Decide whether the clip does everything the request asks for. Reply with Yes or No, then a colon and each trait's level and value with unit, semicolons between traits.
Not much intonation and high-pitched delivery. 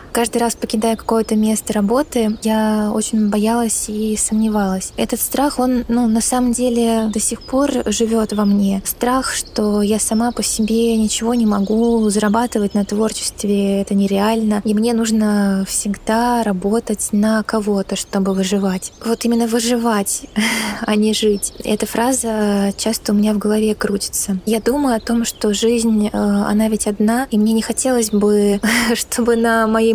Yes: narrow, 1.8 semitones; high, 220 Hz